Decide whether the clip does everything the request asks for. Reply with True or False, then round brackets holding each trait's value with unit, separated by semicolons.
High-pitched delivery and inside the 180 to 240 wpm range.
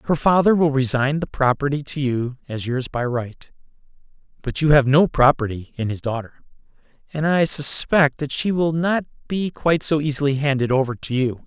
False (140 Hz; 185 wpm)